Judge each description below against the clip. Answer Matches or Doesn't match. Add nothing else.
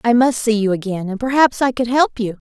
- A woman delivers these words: Matches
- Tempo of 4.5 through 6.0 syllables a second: Matches